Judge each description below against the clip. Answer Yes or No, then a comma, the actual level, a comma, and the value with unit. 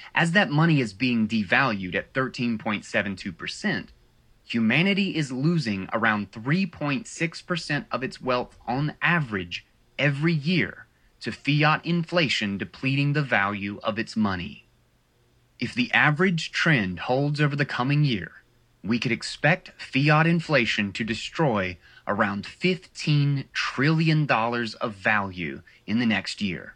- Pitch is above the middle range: No, low, 130 Hz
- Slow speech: Yes, slow, 120 wpm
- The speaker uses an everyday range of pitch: No, wide, 6.1 semitones